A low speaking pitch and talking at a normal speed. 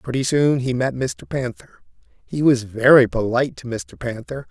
Yes: low, 120 Hz; average, 175 wpm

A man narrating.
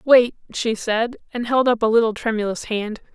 No: female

